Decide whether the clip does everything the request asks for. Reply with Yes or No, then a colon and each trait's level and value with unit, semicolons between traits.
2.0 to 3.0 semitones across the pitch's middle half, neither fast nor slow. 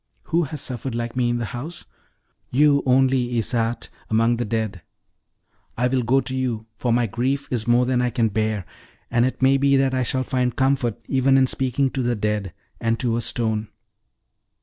Yes: narrow, 2.4 semitones; average, 195 wpm